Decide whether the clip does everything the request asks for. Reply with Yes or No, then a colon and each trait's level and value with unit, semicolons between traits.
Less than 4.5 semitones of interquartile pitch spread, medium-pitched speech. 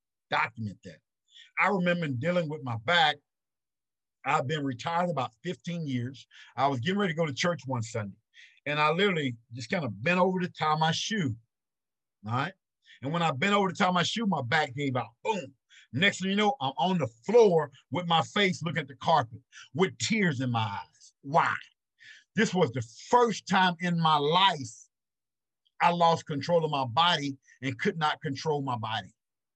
No: wide, 5.4 semitones; medium, 155 Hz